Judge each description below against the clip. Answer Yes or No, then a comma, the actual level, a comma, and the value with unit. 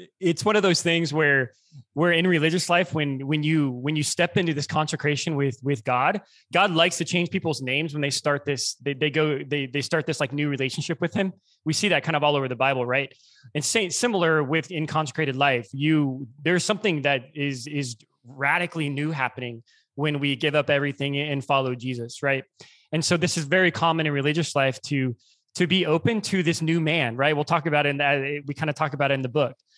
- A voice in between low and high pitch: Yes, medium, 150 Hz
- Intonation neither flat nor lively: Yes, average, 3.1 semitones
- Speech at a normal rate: No, fast, 225 wpm